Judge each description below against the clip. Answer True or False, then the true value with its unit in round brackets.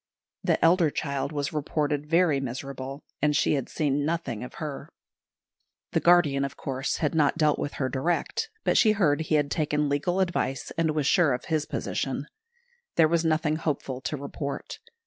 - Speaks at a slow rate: False (175 wpm)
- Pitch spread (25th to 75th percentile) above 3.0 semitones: False (2.6 semitones)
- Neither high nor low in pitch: True (150 Hz)